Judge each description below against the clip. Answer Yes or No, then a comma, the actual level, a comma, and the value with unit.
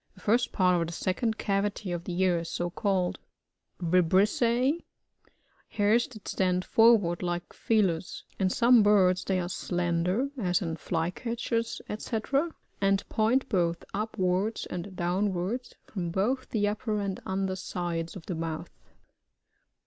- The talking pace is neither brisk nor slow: Yes, average, 150 wpm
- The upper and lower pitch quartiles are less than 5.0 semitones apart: Yes, average, 3.7 semitones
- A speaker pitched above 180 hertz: Yes, high, 190 Hz